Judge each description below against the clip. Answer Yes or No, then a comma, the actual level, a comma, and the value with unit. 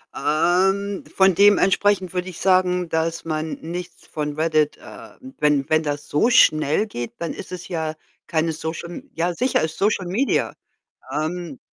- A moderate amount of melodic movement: Yes, average, 3.1 semitones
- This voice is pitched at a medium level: Yes, medium, 170 Hz